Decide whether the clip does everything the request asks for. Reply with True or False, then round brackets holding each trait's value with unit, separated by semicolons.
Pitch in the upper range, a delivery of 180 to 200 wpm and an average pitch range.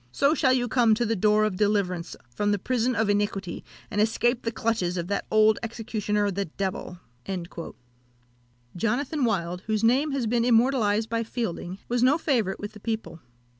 False (220 Hz; 170 wpm; 3.0 semitones)